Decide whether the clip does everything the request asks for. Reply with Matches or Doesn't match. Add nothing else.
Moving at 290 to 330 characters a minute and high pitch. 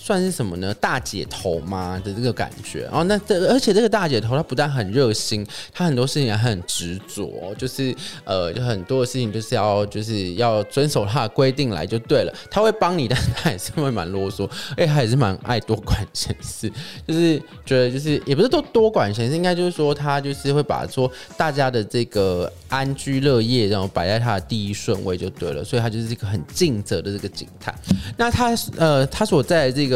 Doesn't match